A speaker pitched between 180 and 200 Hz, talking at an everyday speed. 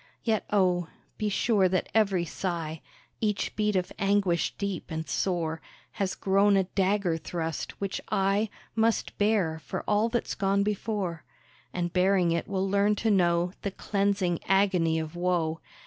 Yes: high, 190 Hz; average, 150 wpm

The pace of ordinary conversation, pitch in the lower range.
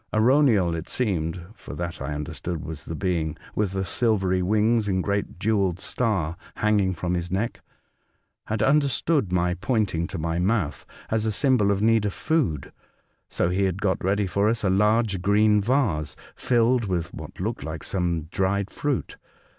Yes: average, 170 wpm; low, 100 Hz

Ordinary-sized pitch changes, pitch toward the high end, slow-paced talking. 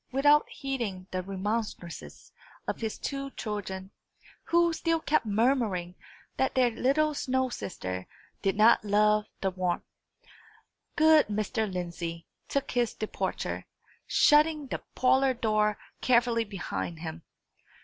No: wide, 5.9 semitones; high, 220 Hz; slow, 120 wpm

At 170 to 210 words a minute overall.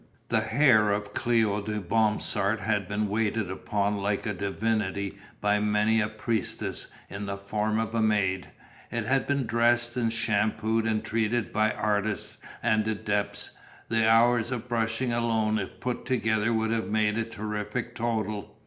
No: average, 160 wpm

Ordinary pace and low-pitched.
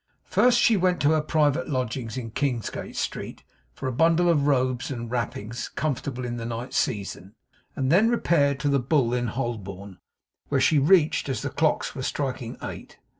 Yes: average, 175 wpm; low, 130 Hz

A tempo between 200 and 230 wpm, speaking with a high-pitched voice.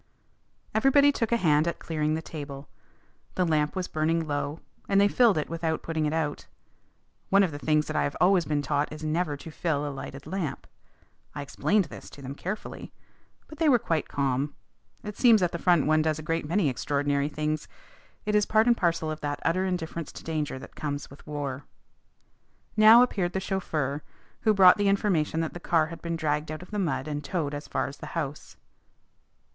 No: fast, 205 wpm; medium, 160 Hz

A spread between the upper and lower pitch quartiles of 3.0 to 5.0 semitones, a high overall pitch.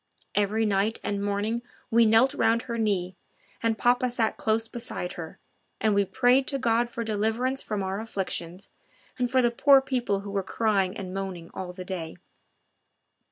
Yes: average, 3.3 semitones; high, 220 Hz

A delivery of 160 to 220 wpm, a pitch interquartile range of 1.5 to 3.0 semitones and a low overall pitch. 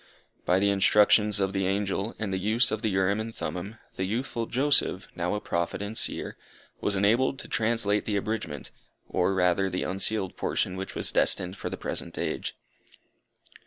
Yes: average, 175 wpm; narrow, 2.6 semitones; low, 100 Hz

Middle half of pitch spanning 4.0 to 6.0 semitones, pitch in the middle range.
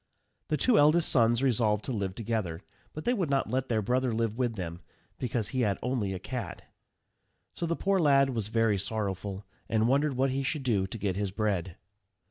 No: average, 4.7 semitones; low, 115 Hz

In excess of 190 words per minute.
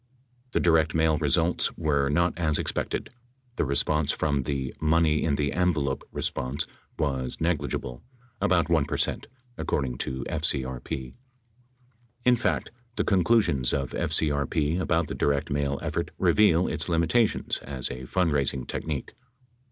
No: slow, 135 wpm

